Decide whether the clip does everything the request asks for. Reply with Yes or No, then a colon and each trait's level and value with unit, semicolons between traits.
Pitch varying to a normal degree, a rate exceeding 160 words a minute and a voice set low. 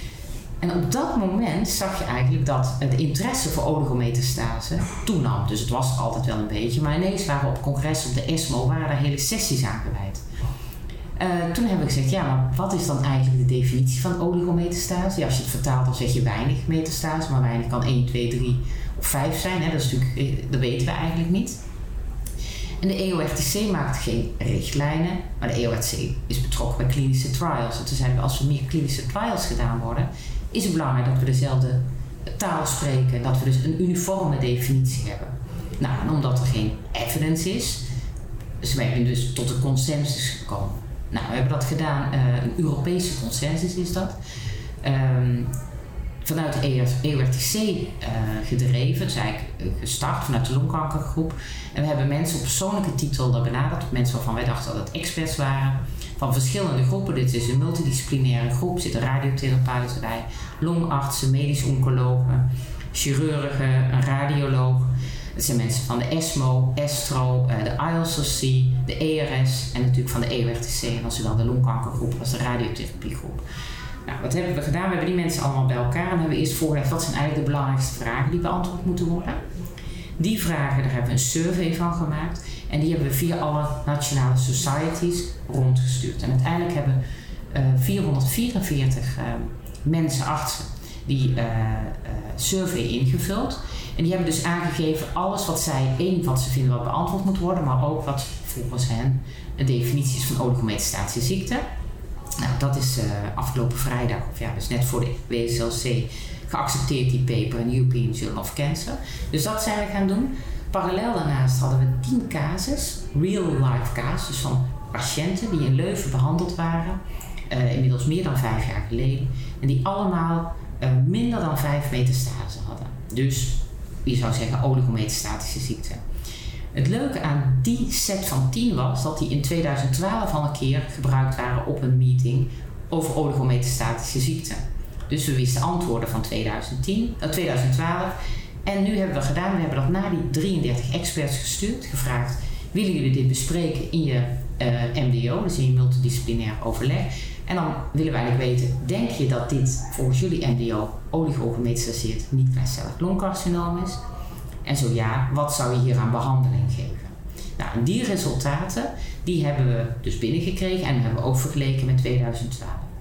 Yes: average, 3.9 semitones; average, 170 wpm; low, 130 Hz